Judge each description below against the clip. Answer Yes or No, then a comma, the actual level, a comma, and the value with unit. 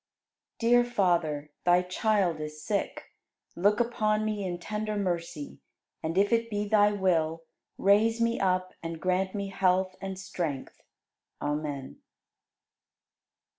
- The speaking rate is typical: No, slow, 130 wpm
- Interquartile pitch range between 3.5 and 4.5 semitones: Yes, average, 4.0 semitones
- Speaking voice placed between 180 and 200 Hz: Yes, high, 190 Hz